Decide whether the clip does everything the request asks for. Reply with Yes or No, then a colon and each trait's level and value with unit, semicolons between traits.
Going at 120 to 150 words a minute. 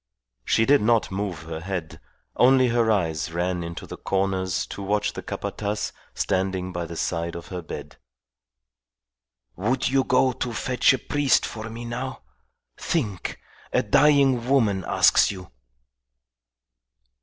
Yes: average, 140 wpm